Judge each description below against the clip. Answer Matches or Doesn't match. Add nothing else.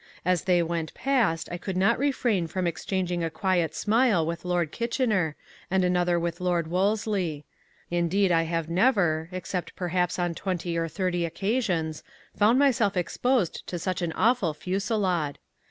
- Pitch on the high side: Doesn't match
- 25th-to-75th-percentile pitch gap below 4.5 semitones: Matches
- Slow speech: Doesn't match